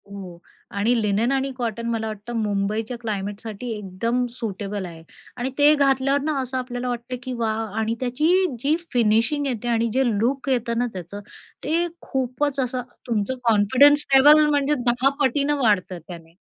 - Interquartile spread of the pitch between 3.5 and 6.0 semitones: Yes, average, 4.1 semitones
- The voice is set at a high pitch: Yes, high, 240 Hz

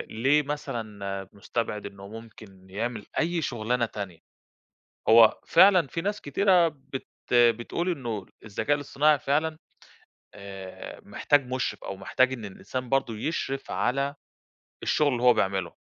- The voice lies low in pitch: Yes, low, 120 Hz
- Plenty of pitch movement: Yes, wide, 5.8 semitones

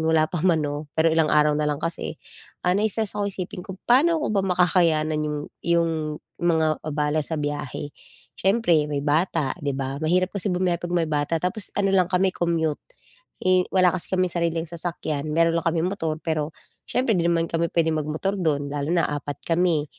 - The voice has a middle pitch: Yes, medium, 165 Hz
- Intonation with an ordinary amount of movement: Yes, average, 3.0 semitones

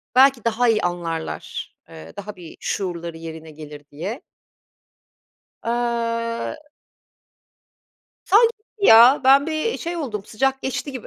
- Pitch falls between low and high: No, high, 230 Hz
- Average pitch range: No, wide, 7.7 semitones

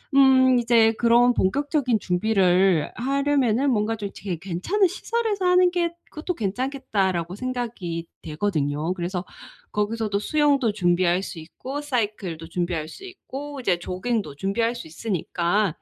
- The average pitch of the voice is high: Yes, high, 220 Hz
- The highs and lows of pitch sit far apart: Yes, wide, 6.8 semitones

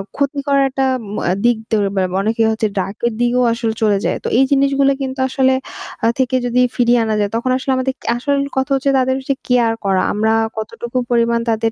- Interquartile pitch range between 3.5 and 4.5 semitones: No, average, 3.0 semitones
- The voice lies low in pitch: No, high, 245 Hz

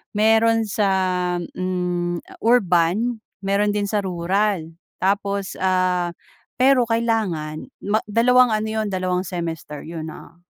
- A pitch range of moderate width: Yes, average, 3.6 semitones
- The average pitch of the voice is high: Yes, high, 195 Hz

